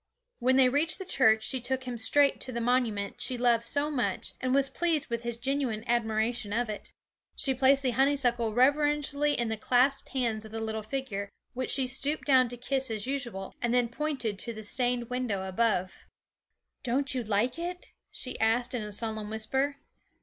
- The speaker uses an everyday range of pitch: Yes, average, 3.3 semitones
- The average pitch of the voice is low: No, high, 245 Hz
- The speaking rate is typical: Yes, average, 190 wpm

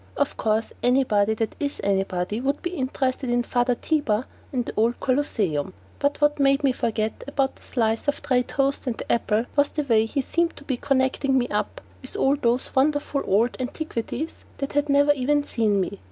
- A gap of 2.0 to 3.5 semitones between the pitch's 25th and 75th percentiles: No, average, 4.0 semitones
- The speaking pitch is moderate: No, very high, 260 Hz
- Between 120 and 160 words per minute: No, average, 195 wpm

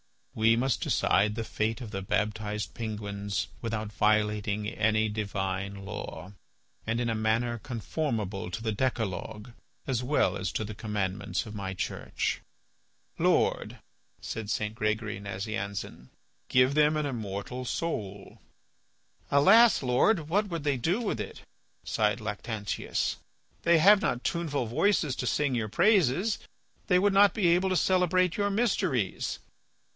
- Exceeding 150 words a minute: No, average, 140 wpm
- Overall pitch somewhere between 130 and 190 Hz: No, low, 110 Hz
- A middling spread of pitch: No, wide, 6.1 semitones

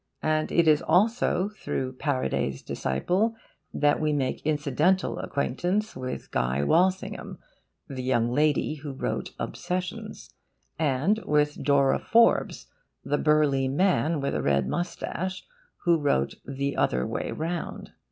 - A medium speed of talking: No, slow, 125 wpm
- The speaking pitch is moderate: Yes, medium, 150 Hz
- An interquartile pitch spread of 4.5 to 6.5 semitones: Yes, average, 5.1 semitones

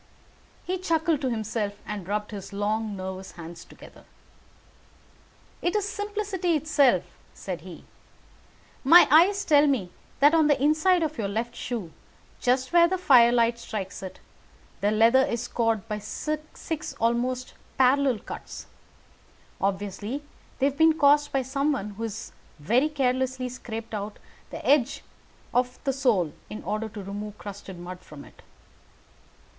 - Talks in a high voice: Yes, high, 245 Hz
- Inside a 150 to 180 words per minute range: No, average, 140 wpm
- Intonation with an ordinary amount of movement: No, wide, 5.9 semitones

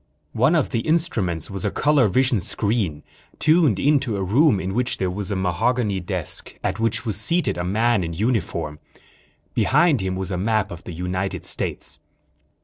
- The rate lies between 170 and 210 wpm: Yes, average, 180 wpm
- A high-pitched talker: No, low, 100 Hz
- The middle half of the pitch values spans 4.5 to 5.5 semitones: Yes, average, 5.2 semitones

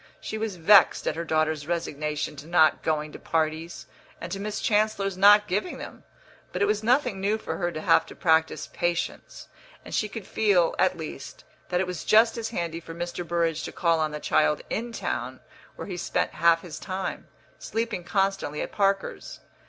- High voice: No, medium, 175 Hz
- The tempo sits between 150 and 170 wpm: No, average, 190 wpm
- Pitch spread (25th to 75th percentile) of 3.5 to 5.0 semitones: Yes, average, 4.2 semitones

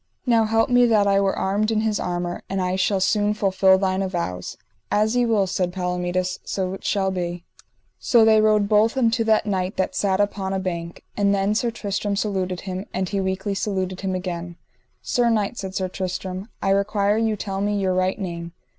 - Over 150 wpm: Yes, average, 200 wpm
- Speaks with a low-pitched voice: No, high, 195 Hz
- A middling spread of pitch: No, narrow, 2.3 semitones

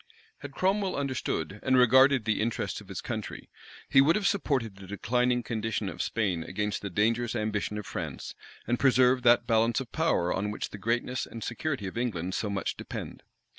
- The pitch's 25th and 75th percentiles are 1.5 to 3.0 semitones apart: No, average, 3.8 semitones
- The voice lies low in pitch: Yes, low, 115 Hz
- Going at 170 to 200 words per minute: Yes, average, 185 wpm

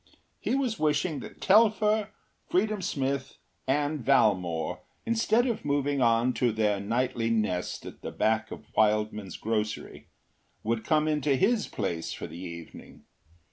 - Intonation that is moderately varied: No, wide, 6.8 semitones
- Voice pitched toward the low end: Yes, low, 130 Hz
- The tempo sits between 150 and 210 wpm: No, average, 140 wpm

